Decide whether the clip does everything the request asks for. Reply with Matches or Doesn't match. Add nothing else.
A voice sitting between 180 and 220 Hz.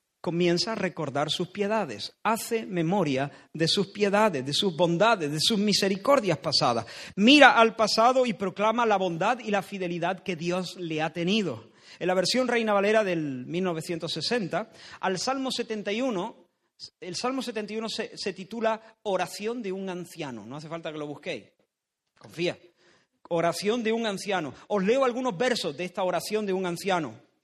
Matches